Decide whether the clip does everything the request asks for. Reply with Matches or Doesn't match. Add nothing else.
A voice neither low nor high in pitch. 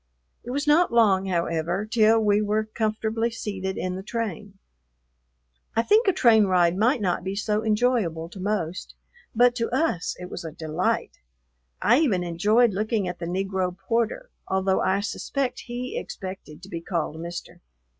Doesn't match